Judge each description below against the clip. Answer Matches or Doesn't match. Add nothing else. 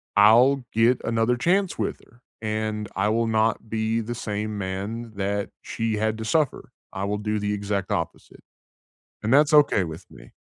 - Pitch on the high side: Doesn't match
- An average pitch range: Doesn't match